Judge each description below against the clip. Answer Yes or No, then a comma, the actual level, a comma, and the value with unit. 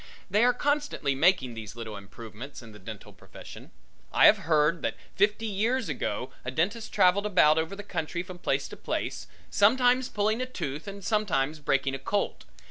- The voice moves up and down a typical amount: No, wide, 7.6 semitones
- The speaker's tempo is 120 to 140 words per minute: No, average, 180 wpm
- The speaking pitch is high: No, medium, 180 Hz